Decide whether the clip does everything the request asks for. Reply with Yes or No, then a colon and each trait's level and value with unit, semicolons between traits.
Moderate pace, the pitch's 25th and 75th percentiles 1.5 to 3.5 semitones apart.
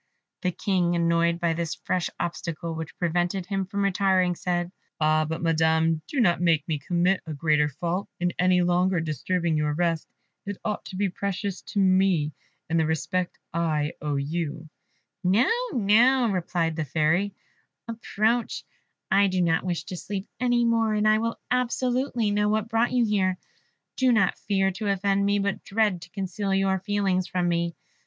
Yes: average, 170 wpm; average, 3.2 semitones